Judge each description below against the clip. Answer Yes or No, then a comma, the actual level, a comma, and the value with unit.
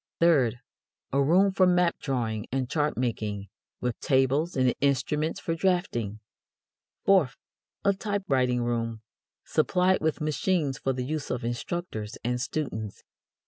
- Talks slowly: Yes, slow, 130 wpm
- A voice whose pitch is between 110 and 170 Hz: Yes, low, 135 Hz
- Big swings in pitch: Yes, wide, 5.8 semitones